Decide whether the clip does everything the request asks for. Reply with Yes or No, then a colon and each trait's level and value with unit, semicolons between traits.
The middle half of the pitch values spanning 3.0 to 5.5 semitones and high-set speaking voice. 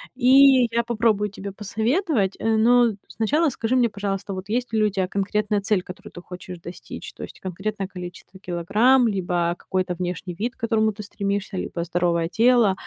Yes: average, 3.9 semitones; high, 205 Hz